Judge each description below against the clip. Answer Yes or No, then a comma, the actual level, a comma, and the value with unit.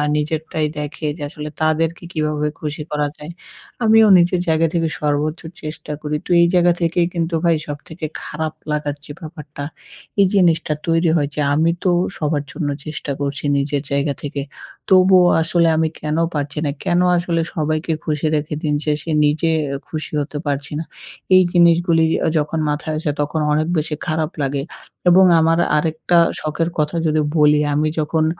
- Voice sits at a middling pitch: Yes, medium, 155 Hz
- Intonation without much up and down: Yes, narrow, 1.9 semitones